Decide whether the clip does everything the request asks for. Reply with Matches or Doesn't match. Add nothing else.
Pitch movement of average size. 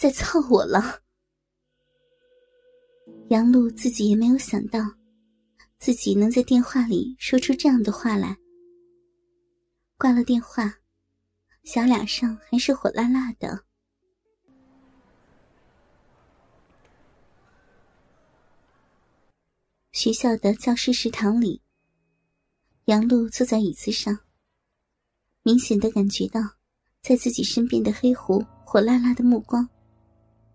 Matches